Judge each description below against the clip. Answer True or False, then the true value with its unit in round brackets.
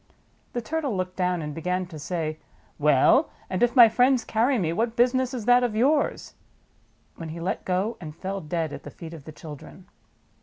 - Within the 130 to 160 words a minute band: False (195 wpm)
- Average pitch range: False (6.9 semitones)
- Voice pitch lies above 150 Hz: True (185 Hz)